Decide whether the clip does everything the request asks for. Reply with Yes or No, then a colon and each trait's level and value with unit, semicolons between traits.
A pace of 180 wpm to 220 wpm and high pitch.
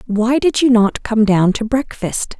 Yes: average, 200 wpm; high, 230 Hz